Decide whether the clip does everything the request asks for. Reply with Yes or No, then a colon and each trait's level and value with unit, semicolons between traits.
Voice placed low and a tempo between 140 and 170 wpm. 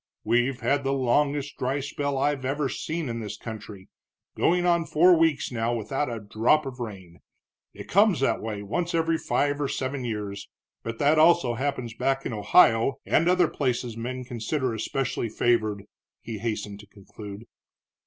Yes: low, 130 Hz; average, 165 wpm